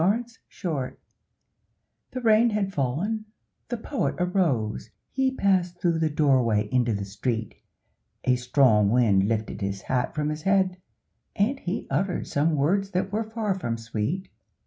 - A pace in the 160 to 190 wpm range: No, average, 150 wpm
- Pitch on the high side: No, medium, 160 Hz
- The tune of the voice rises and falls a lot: Yes, wide, 8.3 semitones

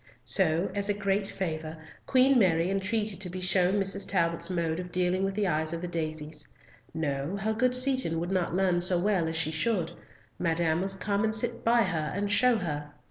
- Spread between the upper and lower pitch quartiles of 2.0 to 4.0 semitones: Yes, average, 3.7 semitones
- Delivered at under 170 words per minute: No, average, 200 wpm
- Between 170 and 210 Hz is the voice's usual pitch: Yes, medium, 185 Hz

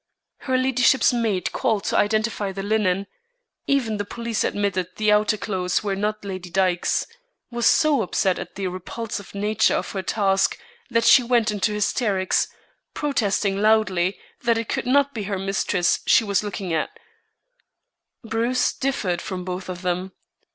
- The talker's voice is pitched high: Yes, high, 205 Hz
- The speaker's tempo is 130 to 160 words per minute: Yes, average, 155 wpm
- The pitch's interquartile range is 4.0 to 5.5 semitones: No, average, 3.4 semitones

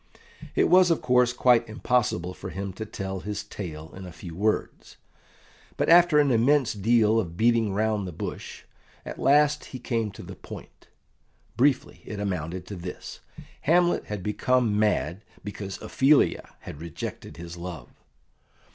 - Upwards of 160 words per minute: No, average, 155 wpm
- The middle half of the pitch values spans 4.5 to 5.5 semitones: Yes, average, 5.1 semitones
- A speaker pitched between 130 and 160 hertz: No, low, 105 Hz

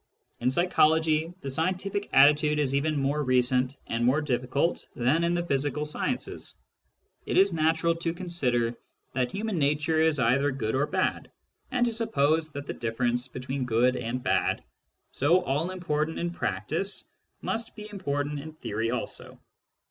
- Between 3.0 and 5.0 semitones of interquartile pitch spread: Yes, average, 4.6 semitones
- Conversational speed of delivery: Yes, average, 155 wpm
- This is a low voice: No, medium, 150 Hz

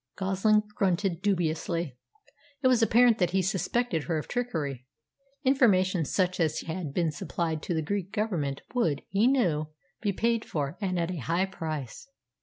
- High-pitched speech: No, medium, 180 Hz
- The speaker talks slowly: No, average, 160 wpm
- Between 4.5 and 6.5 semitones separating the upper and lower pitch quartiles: Yes, average, 4.8 semitones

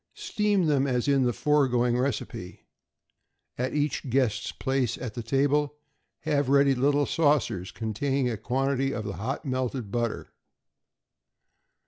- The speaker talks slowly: Yes, slow, 130 wpm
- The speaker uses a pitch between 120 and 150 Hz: Yes, low, 135 Hz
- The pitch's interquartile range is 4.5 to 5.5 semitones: No, average, 2.8 semitones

